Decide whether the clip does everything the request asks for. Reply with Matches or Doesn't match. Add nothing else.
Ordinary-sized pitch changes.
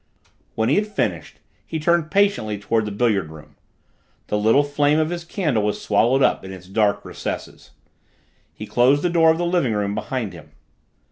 Doesn't match